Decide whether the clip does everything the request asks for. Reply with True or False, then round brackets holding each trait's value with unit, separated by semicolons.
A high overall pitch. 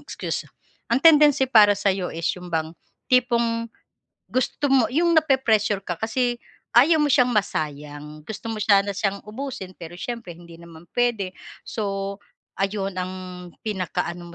True (205 Hz)